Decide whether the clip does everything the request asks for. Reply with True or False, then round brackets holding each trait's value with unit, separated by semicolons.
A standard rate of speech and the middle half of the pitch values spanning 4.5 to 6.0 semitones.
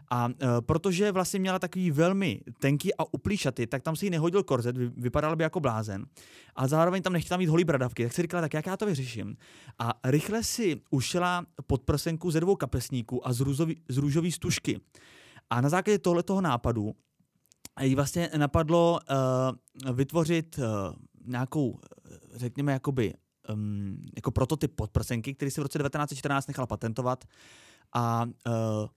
True (155 wpm; 5.5 semitones)